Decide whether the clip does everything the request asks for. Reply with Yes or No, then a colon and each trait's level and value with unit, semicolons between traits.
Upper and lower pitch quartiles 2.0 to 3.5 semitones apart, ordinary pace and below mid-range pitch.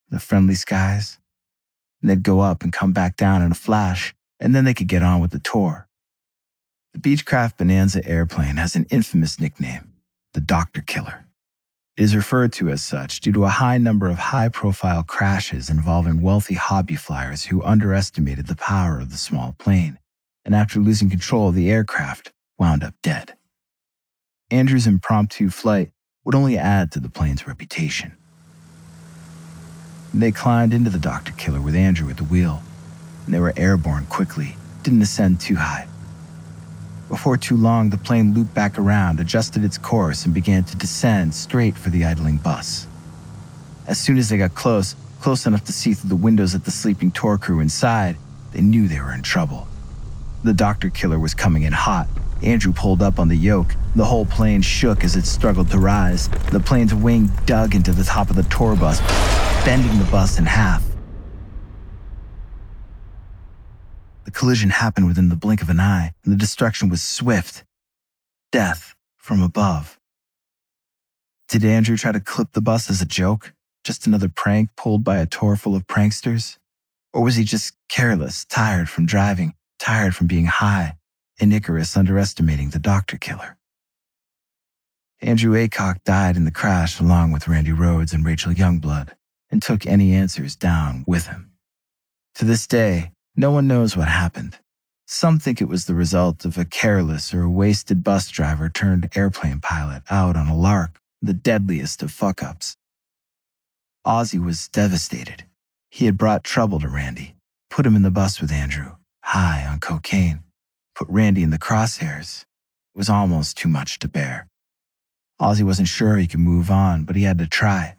No: average, 4.1 semitones; average, 170 wpm; very low, 95 Hz